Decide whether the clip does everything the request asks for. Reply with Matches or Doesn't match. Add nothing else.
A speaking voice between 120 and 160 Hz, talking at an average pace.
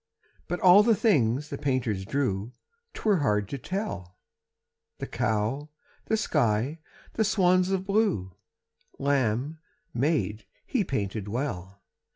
Doesn't match